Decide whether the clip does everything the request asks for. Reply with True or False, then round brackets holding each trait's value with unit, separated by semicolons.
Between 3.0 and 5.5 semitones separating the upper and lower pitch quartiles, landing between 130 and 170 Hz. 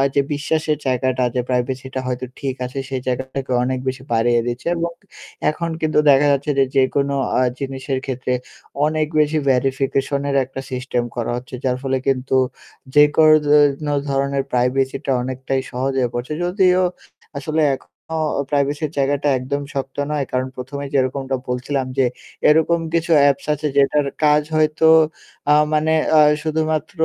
False (2.4 semitones; 135 Hz)